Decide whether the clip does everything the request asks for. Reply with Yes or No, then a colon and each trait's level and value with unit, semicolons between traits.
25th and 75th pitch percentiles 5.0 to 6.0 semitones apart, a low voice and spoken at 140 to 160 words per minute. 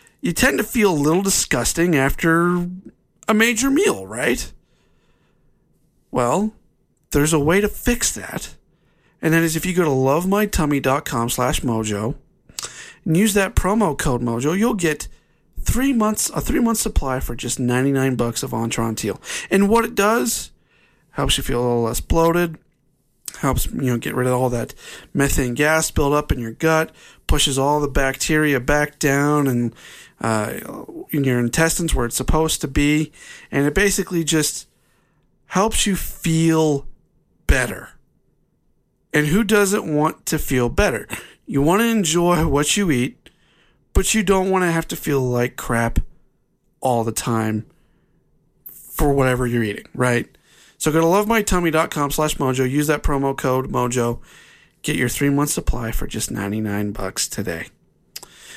No: wide, 5.6 semitones; medium, 150 Hz; average, 155 wpm